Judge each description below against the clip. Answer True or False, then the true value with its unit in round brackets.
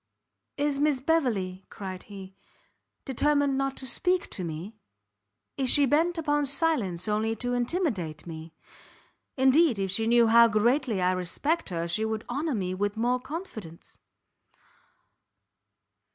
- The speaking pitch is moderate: False (235 Hz)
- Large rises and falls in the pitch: True (7.0 semitones)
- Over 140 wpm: False (135 wpm)